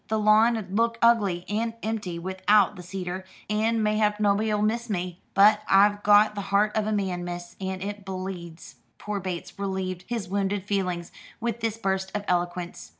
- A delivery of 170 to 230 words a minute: Yes, average, 175 wpm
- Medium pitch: No, high, 200 Hz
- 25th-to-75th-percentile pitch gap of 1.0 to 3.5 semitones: Yes, narrow, 2.4 semitones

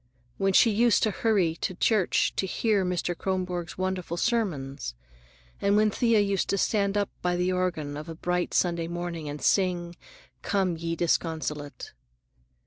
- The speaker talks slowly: No, average, 155 wpm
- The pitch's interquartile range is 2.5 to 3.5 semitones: Yes, average, 3.0 semitones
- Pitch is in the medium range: Yes, medium, 180 Hz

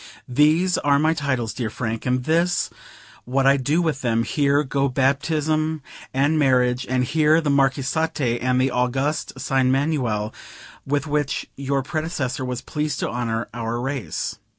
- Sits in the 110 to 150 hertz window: Yes, low, 135 Hz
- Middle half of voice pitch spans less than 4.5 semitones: Yes, average, 3.2 semitones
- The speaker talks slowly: No, average, 150 wpm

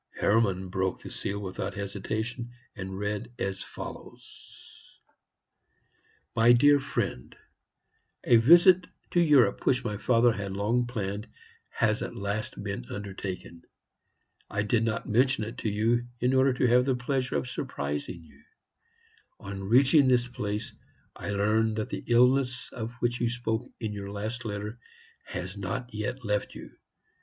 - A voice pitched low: Yes, low, 110 Hz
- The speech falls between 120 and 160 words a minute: Yes, average, 145 wpm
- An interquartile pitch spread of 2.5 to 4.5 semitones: Yes, average, 3.5 semitones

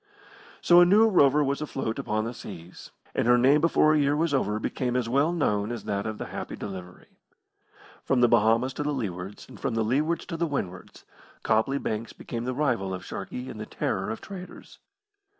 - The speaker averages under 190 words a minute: No, fast, 205 wpm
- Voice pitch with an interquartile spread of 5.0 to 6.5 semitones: Yes, wide, 5.4 semitones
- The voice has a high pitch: No, low, 125 Hz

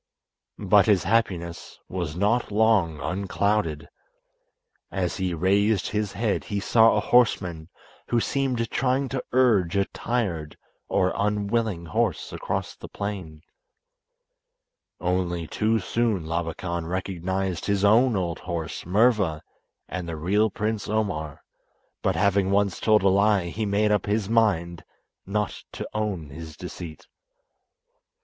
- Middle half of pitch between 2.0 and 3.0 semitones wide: No, average, 3.7 semitones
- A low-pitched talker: Yes, low, 100 Hz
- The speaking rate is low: Yes, slow, 130 wpm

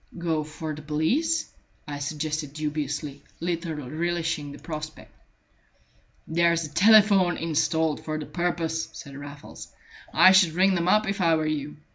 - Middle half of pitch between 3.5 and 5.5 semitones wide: No, narrow, 2.5 semitones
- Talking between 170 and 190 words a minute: No, average, 145 wpm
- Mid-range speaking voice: Yes, medium, 160 Hz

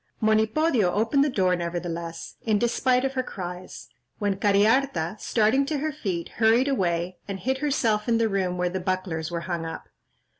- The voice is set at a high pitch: Yes, high, 205 Hz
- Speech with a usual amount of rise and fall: No, wide, 5.7 semitones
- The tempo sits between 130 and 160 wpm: No, average, 180 wpm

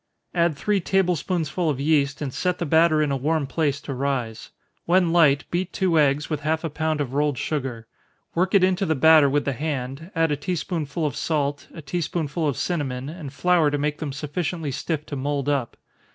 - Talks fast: Yes, fast, 210 wpm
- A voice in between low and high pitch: Yes, medium, 150 Hz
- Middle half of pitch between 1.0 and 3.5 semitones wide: Yes, average, 3.1 semitones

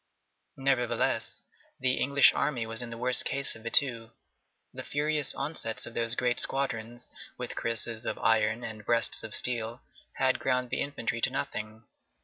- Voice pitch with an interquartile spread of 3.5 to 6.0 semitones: No, average, 2.8 semitones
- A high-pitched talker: No, low, 120 Hz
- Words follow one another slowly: No, average, 160 wpm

